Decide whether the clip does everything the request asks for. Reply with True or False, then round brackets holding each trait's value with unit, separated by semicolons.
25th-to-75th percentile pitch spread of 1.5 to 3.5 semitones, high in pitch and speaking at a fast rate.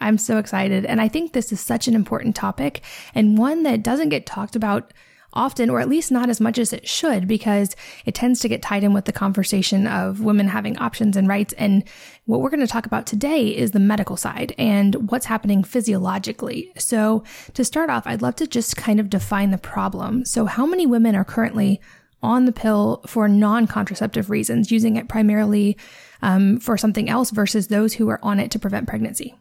True (2.6 semitones; 215 Hz; 210 wpm)